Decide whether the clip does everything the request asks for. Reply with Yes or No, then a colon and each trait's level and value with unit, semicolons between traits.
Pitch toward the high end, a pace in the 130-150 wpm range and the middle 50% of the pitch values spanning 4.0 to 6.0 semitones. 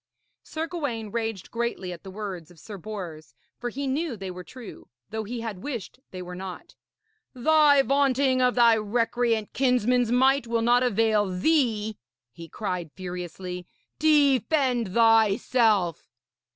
Yes: high, 225 Hz; average, 140 wpm; average, 4.9 semitones